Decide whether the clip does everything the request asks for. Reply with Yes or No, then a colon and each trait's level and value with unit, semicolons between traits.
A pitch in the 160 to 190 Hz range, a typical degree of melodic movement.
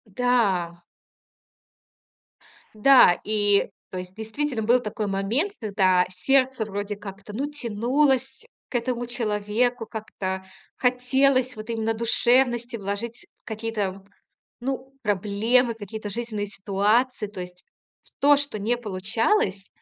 No: high, 220 Hz; average, 3.7 semitones